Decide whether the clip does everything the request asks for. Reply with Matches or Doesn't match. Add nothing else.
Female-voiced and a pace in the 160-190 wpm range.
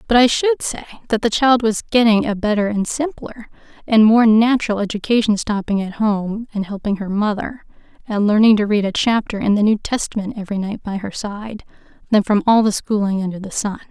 Doesn't match